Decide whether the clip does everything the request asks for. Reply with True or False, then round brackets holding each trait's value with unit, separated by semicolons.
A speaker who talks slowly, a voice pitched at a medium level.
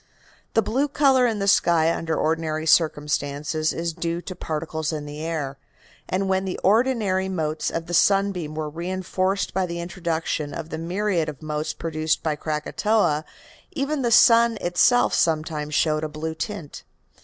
False (160 wpm; 165 Hz)